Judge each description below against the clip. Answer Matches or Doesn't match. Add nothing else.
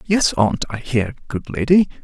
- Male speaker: Matches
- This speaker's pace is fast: Doesn't match